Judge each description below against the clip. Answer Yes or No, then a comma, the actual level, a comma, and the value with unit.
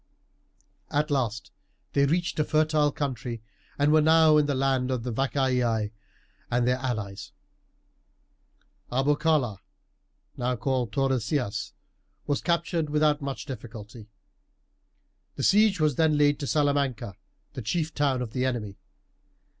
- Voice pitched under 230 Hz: Yes, low, 135 Hz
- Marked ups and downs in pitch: No, average, 3.7 semitones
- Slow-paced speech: Yes, slow, 125 wpm